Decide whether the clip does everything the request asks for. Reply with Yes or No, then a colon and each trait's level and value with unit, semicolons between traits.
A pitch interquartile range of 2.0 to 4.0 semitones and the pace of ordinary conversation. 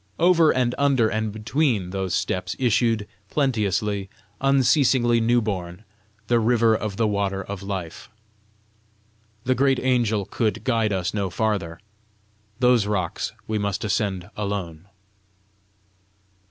No: average, 3.7 semitones; slow, 120 wpm